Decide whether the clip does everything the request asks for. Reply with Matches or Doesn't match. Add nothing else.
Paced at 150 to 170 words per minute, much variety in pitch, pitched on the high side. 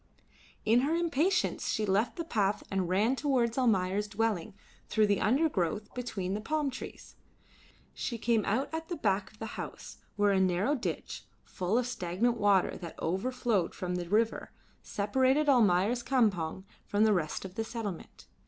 Doesn't match